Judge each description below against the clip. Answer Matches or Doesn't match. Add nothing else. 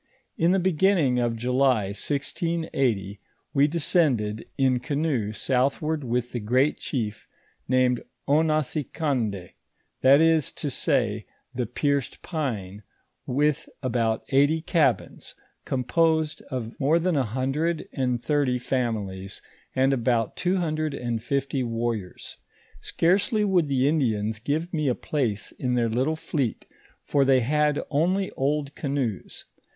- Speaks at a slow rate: Matches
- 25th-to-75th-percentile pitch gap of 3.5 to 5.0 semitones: Matches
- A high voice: Doesn't match